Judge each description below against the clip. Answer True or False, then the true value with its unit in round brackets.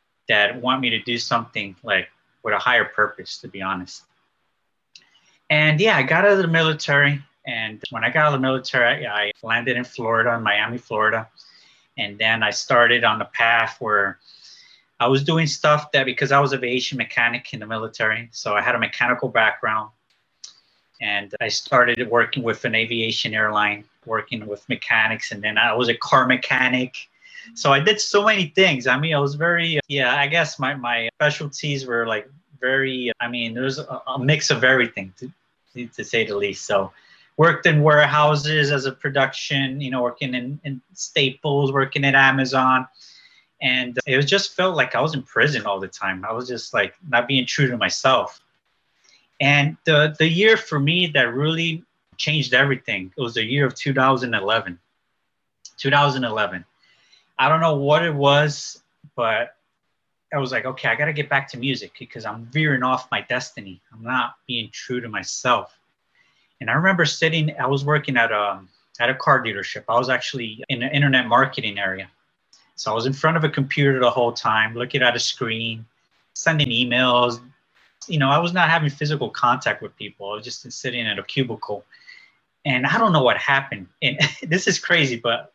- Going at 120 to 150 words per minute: False (190 wpm)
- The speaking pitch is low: True (130 Hz)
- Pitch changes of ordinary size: True (4.0 semitones)